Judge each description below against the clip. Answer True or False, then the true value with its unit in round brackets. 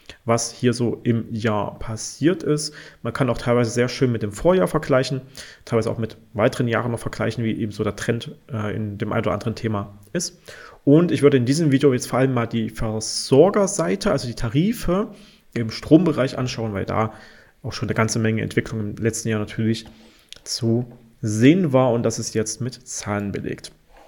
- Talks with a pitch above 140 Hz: False (115 Hz)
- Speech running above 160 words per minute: True (190 wpm)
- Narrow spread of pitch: False (3.3 semitones)